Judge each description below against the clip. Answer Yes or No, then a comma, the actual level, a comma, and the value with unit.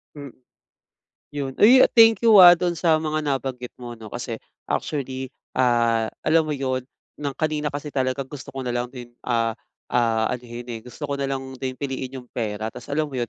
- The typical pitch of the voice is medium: No, low, 130 Hz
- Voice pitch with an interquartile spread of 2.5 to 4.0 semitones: Yes, average, 3.5 semitones